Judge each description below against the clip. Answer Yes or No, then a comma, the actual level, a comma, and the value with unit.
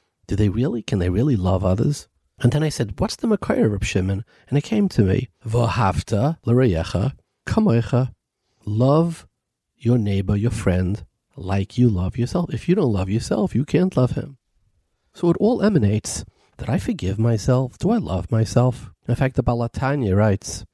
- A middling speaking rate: Yes, average, 170 wpm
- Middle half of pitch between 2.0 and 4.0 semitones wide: No, average, 4.8 semitones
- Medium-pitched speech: No, low, 115 Hz